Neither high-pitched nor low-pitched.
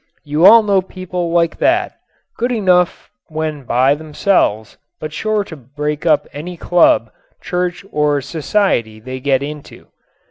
Yes: medium, 155 Hz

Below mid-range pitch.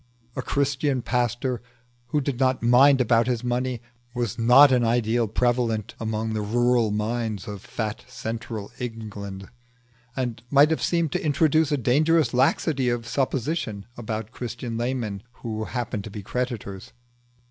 Yes: low, 120 Hz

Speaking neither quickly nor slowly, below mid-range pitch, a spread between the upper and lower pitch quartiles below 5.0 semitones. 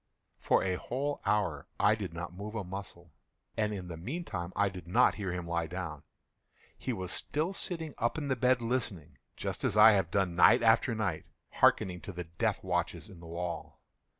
Yes: average, 190 wpm; very low, 95 Hz; average, 4.6 semitones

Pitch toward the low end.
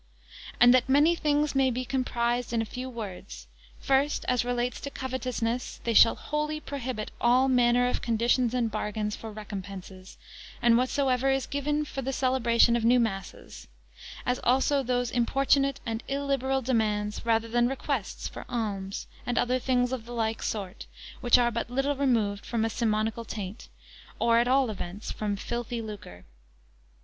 No: high, 240 Hz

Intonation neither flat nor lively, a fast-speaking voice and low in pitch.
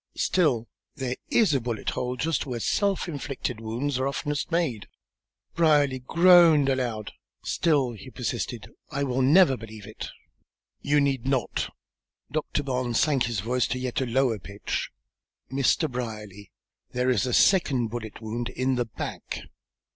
No: average, 3.5 semitones; average, 145 wpm; low, 130 Hz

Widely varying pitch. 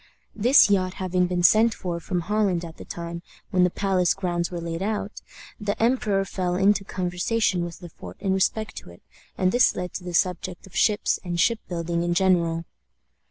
No: narrow, 2.6 semitones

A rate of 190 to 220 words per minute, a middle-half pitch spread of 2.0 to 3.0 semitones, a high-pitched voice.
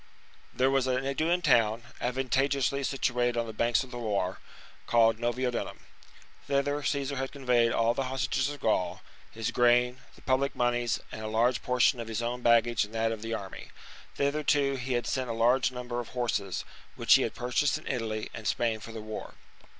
No: average, 195 wpm; average, 2.7 semitones; low, 120 Hz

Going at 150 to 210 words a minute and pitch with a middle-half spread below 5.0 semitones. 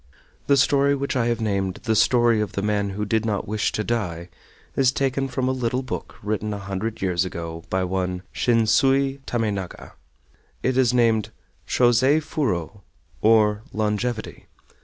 Yes: average, 160 wpm; average, 4.1 semitones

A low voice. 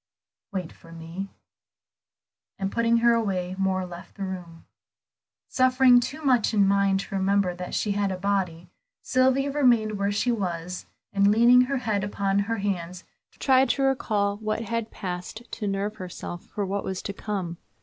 No: high, 200 Hz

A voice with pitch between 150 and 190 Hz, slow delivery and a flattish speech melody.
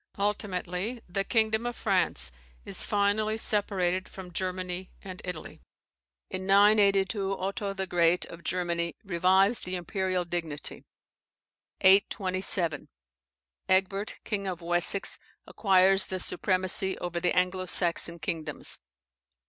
Yes: medium, 185 Hz; slow, 110 wpm; narrow, 1.9 semitones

